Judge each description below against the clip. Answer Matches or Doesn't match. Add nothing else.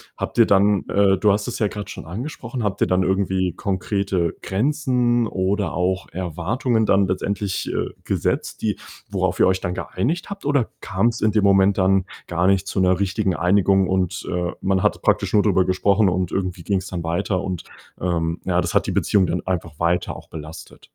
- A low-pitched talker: Matches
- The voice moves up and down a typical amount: Doesn't match